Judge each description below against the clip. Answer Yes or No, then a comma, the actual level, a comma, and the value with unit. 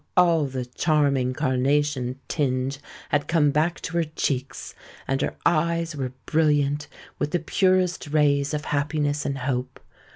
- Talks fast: No, average, 140 wpm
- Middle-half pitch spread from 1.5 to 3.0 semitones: Yes, narrow, 2.6 semitones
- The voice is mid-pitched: Yes, medium, 145 Hz